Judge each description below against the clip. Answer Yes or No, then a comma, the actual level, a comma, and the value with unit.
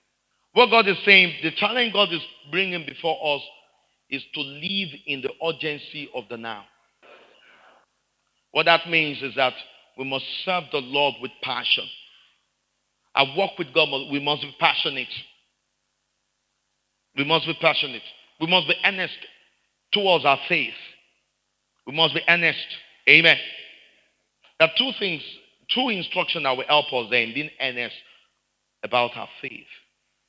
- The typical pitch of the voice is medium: Yes, medium, 155 Hz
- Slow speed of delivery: No, average, 145 wpm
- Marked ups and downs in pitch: No, average, 4.3 semitones